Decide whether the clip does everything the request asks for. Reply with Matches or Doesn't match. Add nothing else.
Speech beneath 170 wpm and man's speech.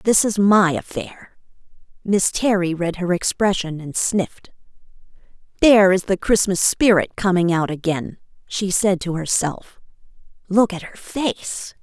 Doesn't match